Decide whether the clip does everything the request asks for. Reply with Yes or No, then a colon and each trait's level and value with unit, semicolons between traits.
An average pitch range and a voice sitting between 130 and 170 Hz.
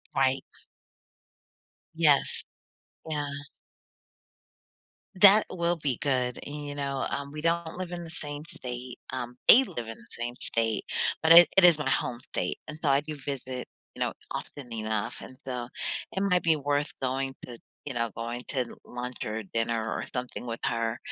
Yes: average, 4.0 semitones; low, 135 Hz